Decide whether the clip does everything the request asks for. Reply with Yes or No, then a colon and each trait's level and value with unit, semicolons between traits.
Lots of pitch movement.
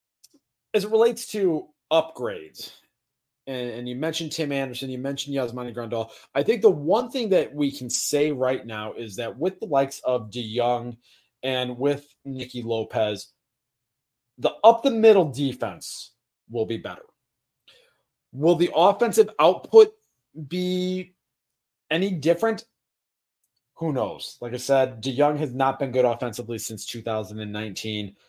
Yes: wide, 6.4 semitones